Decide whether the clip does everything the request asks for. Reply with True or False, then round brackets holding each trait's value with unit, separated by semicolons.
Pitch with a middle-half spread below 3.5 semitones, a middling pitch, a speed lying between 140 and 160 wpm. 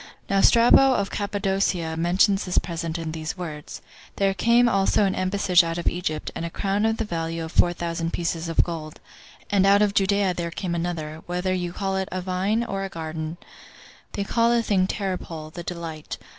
False (3.1 semitones; 180 Hz; 195 wpm)